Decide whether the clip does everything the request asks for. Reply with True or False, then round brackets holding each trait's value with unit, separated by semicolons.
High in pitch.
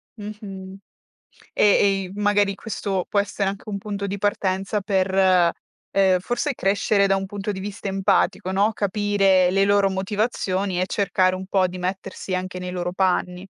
True (195 Hz)